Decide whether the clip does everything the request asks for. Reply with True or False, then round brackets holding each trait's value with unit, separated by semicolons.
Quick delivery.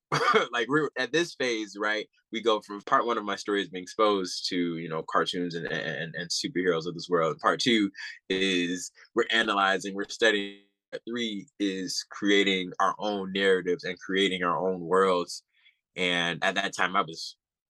False (175 wpm)